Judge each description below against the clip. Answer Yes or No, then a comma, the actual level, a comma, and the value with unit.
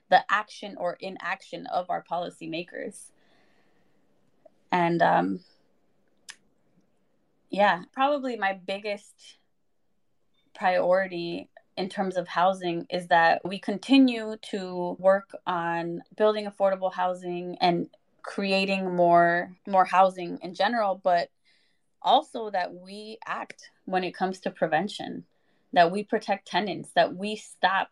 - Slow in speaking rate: Yes, slow, 110 wpm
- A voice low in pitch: No, high, 190 Hz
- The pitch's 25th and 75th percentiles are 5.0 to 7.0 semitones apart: No, average, 3.0 semitones